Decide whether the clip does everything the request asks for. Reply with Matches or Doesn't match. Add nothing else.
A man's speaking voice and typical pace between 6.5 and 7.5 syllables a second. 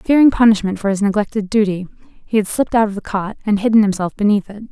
Doesn't match